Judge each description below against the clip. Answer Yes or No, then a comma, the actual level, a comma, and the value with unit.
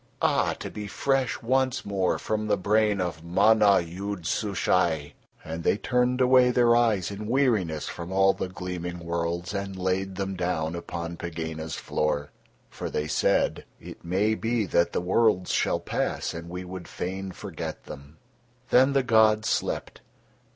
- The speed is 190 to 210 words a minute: No, average, 160 wpm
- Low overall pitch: Yes, very low, 95 Hz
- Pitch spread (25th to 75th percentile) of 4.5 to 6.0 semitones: No, average, 4.1 semitones